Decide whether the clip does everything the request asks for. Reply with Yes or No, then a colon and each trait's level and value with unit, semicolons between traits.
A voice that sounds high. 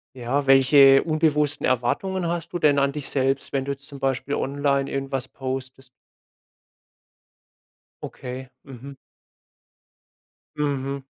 No: medium, 140 Hz